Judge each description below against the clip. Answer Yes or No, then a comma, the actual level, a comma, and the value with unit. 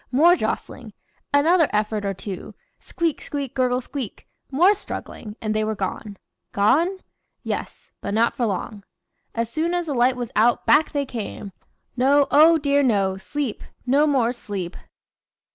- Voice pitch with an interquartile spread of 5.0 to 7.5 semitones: Yes, average, 5.3 semitones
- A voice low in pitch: No, very high, 250 Hz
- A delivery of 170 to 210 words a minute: No, average, 155 wpm